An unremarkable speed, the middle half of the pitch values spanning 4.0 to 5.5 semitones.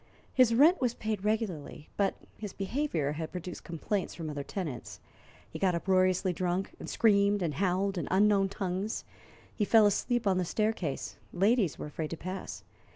No: average, 170 wpm; average, 3.3 semitones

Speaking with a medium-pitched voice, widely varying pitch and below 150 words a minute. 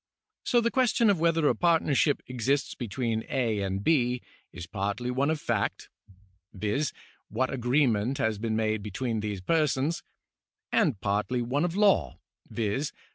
No: low, 125 Hz; wide, 6.0 semitones; average, 140 wpm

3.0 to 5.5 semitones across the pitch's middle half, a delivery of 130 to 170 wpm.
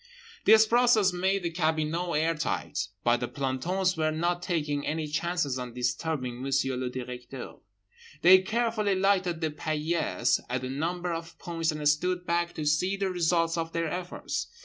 Yes: average, 3.7 semitones; average, 165 wpm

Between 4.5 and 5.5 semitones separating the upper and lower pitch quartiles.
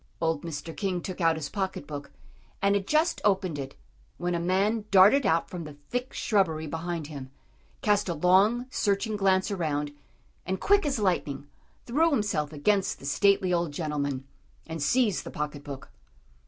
Yes: average, 5.2 semitones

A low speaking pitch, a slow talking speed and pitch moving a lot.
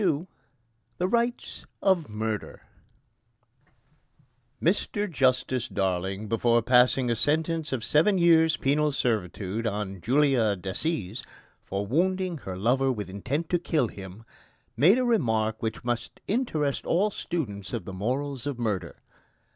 Yes: low, 125 Hz; slow, 130 wpm; wide, 7.3 semitones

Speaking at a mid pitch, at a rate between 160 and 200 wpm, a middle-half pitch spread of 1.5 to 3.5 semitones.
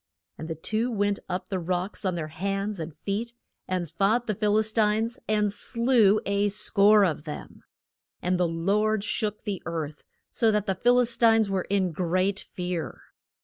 No: high, 200 Hz; average, 185 wpm; average, 3.1 semitones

